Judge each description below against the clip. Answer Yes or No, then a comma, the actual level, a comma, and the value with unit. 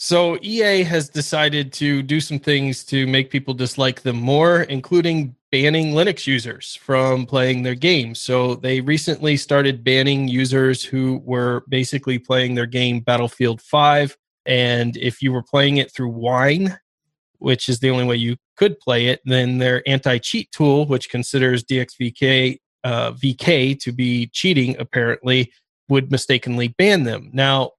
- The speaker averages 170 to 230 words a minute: No, average, 155 wpm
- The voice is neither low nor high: No, low, 130 Hz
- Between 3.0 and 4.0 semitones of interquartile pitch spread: No, narrow, 2.5 semitones